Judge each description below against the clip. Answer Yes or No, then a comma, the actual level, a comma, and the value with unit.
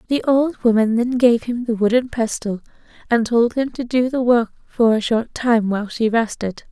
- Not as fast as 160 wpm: No, fast, 205 wpm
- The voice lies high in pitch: Yes, high, 235 Hz